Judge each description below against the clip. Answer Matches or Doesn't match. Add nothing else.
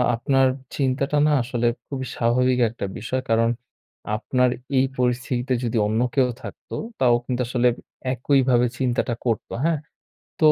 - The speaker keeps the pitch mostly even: Matches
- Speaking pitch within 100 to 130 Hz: Matches